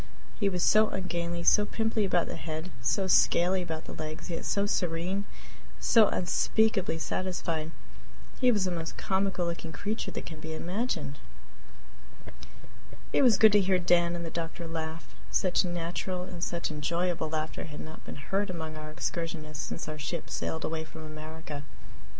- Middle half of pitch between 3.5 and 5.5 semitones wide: No, average, 2.9 semitones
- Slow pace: No, average, 165 wpm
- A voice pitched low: No, medium, 170 Hz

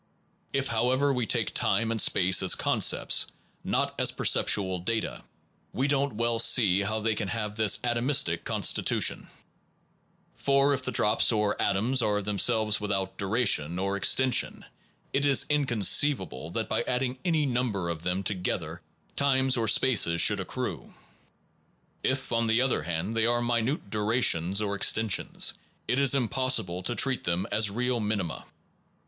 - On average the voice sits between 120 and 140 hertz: No, low, 110 Hz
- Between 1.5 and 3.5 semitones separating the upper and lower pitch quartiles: No, average, 4.5 semitones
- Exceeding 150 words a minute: Yes, average, 170 wpm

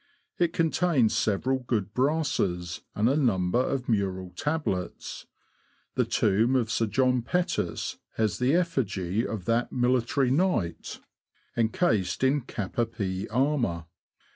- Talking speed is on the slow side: Yes, slow, 130 wpm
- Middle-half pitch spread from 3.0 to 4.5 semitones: No, wide, 5.4 semitones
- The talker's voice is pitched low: Yes, low, 120 Hz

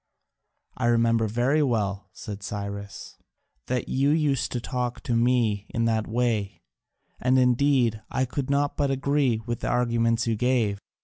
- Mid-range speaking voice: No, low, 120 Hz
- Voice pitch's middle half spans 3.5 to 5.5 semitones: No, average, 2.9 semitones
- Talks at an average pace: Yes, average, 150 wpm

